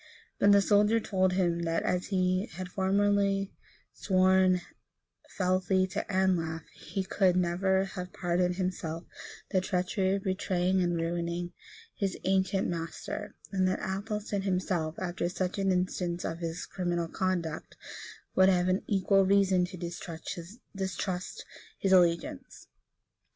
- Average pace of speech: No, slow, 130 wpm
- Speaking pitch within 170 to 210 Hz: Yes, medium, 185 Hz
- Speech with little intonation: Yes, narrow, 1.6 semitones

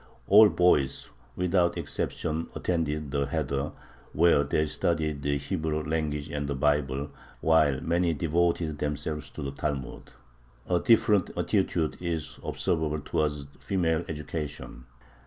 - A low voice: Yes, very low, 75 Hz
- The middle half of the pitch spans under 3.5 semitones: Yes, average, 2.8 semitones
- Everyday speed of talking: No, slow, 120 wpm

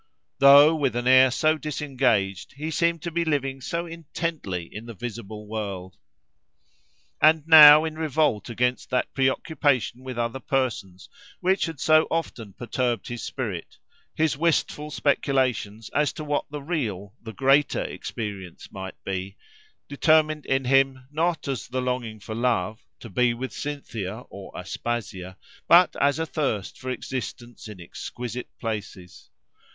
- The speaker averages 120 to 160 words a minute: Yes, average, 140 wpm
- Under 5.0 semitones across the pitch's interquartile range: No, wide, 5.4 semitones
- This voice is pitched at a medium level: No, low, 130 Hz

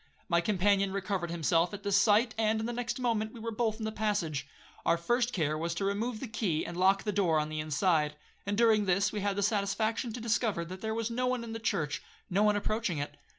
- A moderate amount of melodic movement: Yes, average, 4.1 semitones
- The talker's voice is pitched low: No, high, 205 Hz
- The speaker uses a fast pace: Yes, fast, 240 wpm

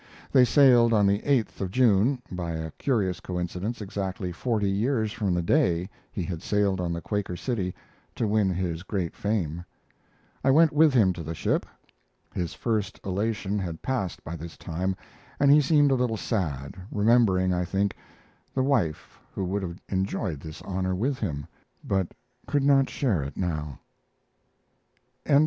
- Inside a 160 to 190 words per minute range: Yes, average, 165 wpm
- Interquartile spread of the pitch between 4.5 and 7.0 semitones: Yes, average, 4.9 semitones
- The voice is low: Yes, very low, 95 Hz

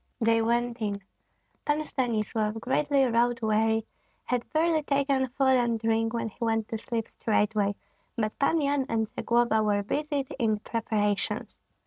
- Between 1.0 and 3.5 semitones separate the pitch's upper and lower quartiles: Yes, average, 3.2 semitones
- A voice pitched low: No, high, 230 Hz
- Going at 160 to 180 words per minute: No, average, 145 wpm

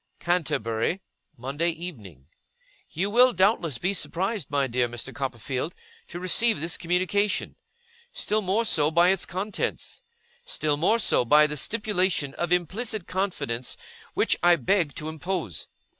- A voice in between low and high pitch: Yes, medium, 170 Hz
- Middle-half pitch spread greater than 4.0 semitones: Yes, average, 5.1 semitones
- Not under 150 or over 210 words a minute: No, slow, 135 wpm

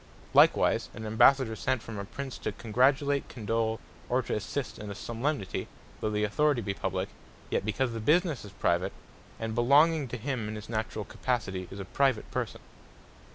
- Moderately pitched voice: No, low, 115 Hz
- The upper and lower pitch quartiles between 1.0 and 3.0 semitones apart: No, average, 4.0 semitones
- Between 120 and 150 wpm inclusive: No, average, 170 wpm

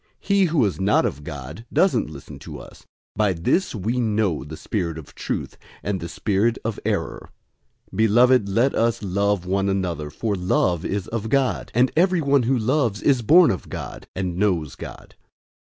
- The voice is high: No, low, 105 Hz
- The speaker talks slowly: No, average, 175 wpm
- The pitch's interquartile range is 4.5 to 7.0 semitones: Yes, wide, 5.4 semitones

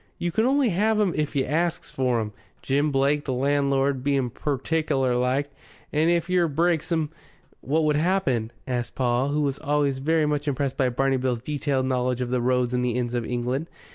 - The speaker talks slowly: No, average, 200 wpm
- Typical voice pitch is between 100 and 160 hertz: Yes, medium, 140 Hz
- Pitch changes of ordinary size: Yes, average, 3.4 semitones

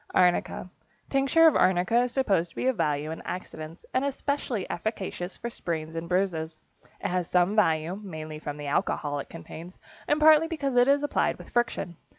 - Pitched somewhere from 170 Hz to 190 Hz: Yes, medium, 185 Hz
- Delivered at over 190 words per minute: No, average, 180 wpm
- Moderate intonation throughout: No, wide, 7.5 semitones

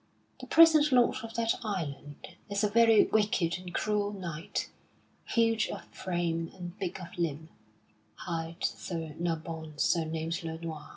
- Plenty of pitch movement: No, average, 4.5 semitones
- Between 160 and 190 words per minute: No, average, 140 wpm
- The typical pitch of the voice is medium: Yes, medium, 175 Hz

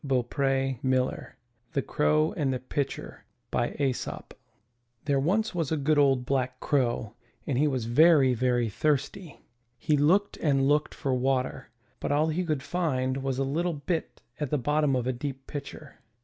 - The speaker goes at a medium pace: Yes, average, 175 wpm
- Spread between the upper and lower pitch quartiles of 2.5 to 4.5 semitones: Yes, average, 2.9 semitones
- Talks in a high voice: No, low, 135 Hz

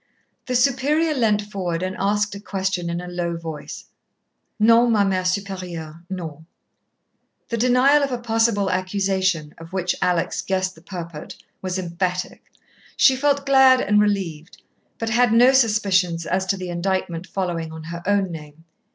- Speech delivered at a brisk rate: No, average, 155 wpm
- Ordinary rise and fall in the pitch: Yes, average, 4.6 semitones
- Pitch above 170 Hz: Yes, high, 190 Hz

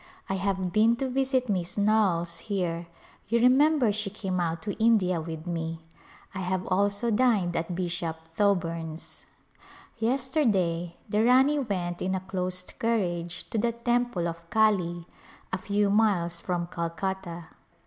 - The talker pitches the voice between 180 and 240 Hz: Yes, high, 190 Hz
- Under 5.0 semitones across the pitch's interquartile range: Yes, average, 4.3 semitones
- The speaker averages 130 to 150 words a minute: Yes, average, 140 wpm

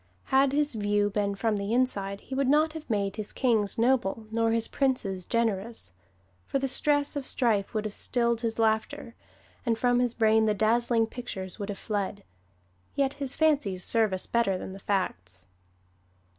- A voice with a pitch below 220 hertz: No, high, 225 Hz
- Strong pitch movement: No, average, 3.9 semitones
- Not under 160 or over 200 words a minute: Yes, average, 175 wpm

